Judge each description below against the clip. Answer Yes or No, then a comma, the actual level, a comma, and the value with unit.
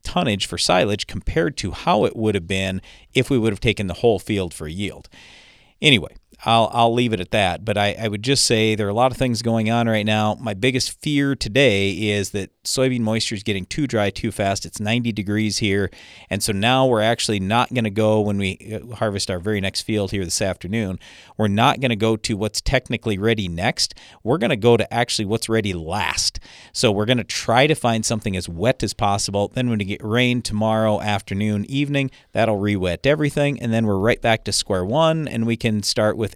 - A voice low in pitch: Yes, low, 110 Hz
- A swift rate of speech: Yes, fast, 225 wpm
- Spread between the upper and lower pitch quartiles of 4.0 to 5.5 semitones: No, average, 2.7 semitones